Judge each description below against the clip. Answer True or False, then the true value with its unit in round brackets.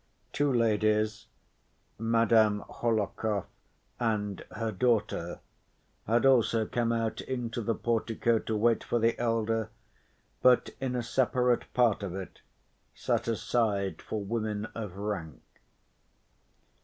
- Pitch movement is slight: True (1.9 semitones)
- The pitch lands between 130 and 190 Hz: False (115 Hz)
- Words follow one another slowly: True (115 wpm)